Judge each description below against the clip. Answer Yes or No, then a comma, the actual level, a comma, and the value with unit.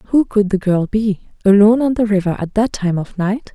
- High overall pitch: Yes, high, 205 Hz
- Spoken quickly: Yes, fast, 235 wpm